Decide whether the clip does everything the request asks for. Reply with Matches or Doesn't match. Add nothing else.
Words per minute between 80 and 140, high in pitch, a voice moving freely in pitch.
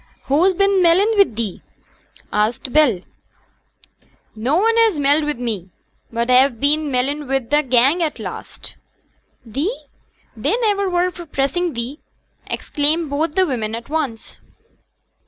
Matches